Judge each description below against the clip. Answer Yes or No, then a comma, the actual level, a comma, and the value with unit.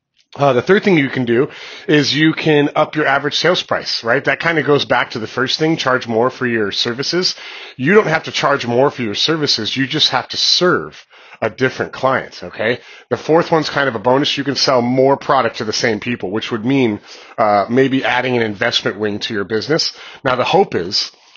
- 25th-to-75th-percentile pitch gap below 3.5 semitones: No, average, 4.1 semitones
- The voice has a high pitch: No, low, 130 Hz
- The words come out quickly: Yes, fast, 225 wpm